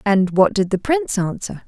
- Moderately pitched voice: No, high, 210 Hz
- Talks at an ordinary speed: No, fast, 215 wpm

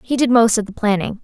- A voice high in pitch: Yes, high, 225 Hz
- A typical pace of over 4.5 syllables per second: Yes, 6.2 syllables/s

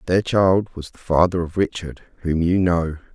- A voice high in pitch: No, very low, 85 Hz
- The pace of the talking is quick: No, average, 190 wpm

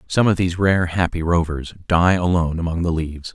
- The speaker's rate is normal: Yes, average, 195 wpm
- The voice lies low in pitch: Yes, very low, 85 Hz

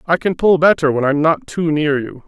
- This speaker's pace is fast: Yes, fast, 265 wpm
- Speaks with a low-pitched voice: No, medium, 155 Hz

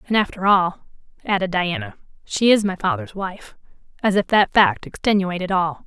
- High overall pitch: Yes, high, 195 Hz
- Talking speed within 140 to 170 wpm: Yes, average, 165 wpm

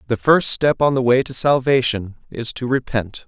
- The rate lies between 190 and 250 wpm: Yes, average, 200 wpm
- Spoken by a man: Yes, male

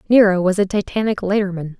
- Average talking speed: Yes, average, 165 wpm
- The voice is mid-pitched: No, high, 195 Hz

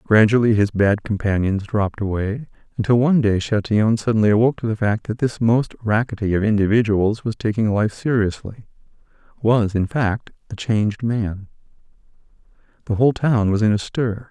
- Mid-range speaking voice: No, low, 110 Hz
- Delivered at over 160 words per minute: No, average, 155 wpm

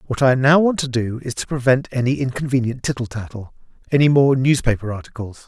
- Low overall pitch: Yes, low, 130 Hz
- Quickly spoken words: No, average, 175 wpm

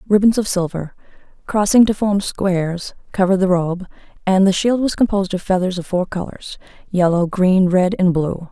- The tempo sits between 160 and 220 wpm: Yes, average, 175 wpm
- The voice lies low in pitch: No, high, 190 Hz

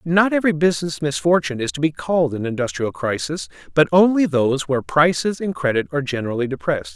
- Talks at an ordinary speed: Yes, average, 180 wpm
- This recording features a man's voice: Yes, male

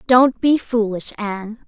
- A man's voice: No, female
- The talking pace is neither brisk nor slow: Yes, average, 145 wpm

